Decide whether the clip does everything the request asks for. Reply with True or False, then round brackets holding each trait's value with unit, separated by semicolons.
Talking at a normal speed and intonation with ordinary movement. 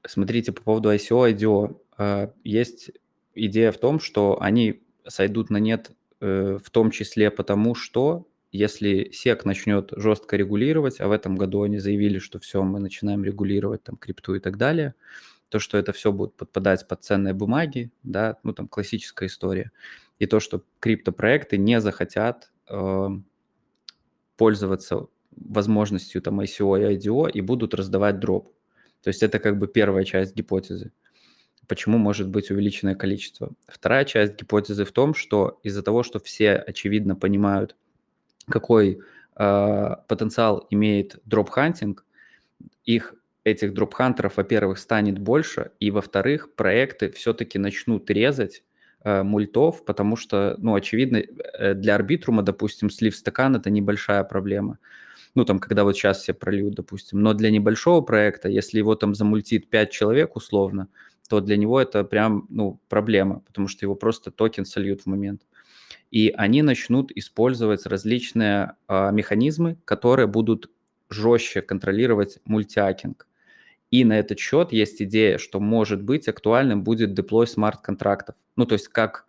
False (145 wpm; 2.0 semitones)